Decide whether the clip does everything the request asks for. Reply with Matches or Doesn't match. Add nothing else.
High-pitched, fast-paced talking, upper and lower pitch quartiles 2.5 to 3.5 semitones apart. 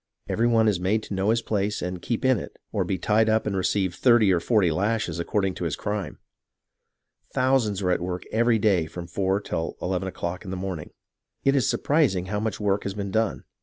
Doesn't match